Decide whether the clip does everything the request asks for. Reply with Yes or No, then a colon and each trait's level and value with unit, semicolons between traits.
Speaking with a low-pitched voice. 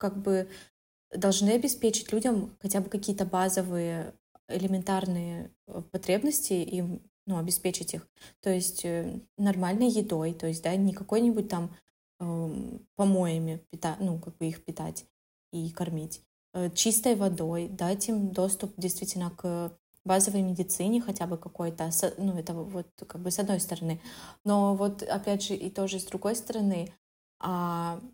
No: medium, 185 Hz